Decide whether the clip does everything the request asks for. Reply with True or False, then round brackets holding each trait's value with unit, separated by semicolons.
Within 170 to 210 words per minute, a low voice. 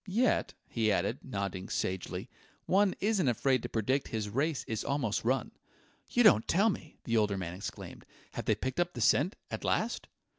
True (180 wpm; 125 Hz)